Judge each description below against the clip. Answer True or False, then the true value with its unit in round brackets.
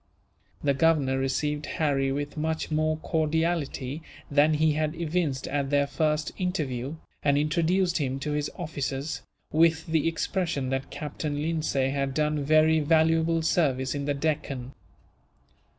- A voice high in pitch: False (150 Hz)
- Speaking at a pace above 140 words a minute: False (135 wpm)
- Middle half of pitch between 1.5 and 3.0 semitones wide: True (2.4 semitones)